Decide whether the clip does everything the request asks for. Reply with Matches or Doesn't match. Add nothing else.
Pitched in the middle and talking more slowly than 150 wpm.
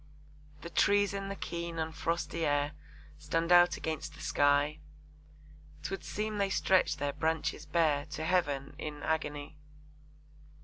Matches